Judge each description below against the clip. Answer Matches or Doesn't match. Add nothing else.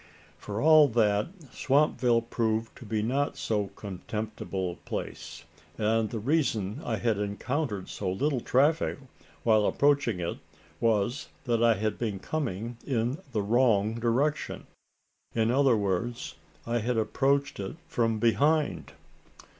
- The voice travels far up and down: Doesn't match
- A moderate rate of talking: Doesn't match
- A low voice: Matches